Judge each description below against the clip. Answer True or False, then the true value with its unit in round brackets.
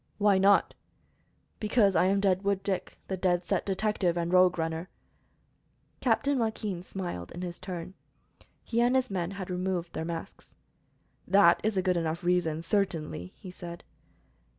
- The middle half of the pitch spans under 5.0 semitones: True (2.6 semitones)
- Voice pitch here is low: False (185 Hz)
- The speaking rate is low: False (155 wpm)